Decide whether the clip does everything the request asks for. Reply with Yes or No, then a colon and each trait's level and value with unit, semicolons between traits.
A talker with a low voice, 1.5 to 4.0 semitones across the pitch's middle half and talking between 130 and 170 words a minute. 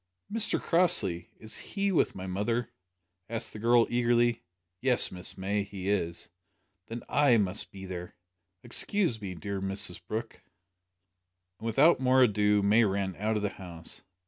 Yes: low, 105 Hz; average, 3.7 semitones; average, 150 wpm